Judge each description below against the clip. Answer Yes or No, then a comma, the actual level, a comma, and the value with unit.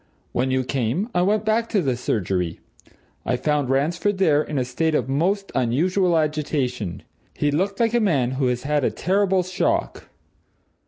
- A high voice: No, medium, 150 Hz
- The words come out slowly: No, average, 170 wpm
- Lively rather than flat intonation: Yes, wide, 6.6 semitones